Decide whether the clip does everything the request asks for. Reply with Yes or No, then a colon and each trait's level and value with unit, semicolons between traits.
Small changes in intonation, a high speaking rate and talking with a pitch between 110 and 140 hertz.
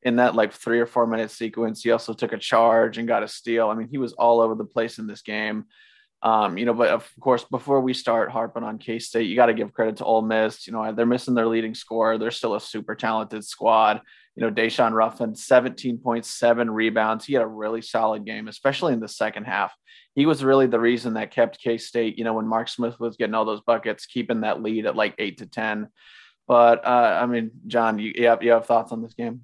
Yes: narrow, 1.2 semitones; fast, 245 wpm; low, 115 Hz